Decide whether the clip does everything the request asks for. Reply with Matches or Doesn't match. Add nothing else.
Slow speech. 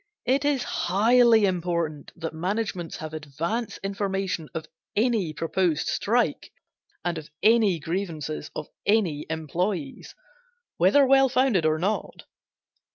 Matches